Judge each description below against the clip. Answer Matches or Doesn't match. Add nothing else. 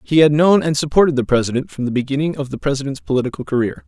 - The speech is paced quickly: Matches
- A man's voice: Matches